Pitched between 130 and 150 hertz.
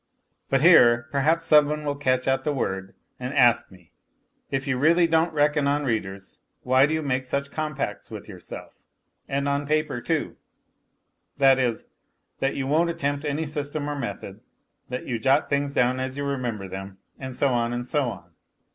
Yes: medium, 140 Hz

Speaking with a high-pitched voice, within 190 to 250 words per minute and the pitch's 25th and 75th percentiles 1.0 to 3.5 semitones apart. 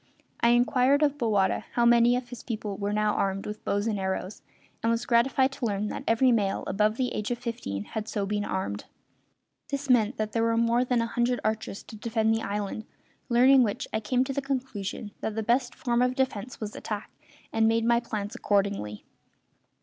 Yes: high, 225 Hz; fast, 205 wpm; average, 2.9 semitones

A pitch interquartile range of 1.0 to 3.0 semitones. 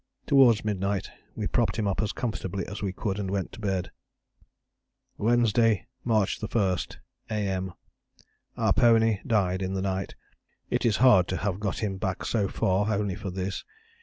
Yes: narrow, 2.6 semitones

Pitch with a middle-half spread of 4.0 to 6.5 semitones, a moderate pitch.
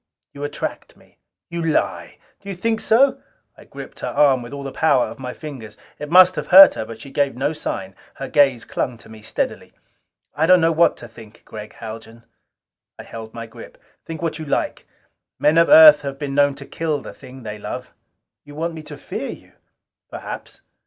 Yes: wide, 5.5 semitones; medium, 145 Hz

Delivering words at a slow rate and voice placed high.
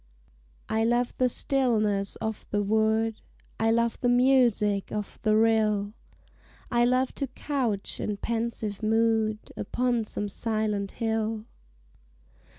Yes: slow, 120 wpm; high, 225 Hz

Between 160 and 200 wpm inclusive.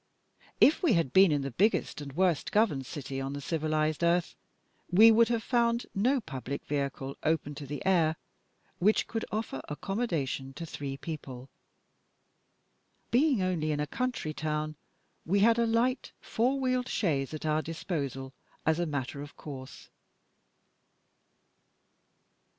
No: average, 145 wpm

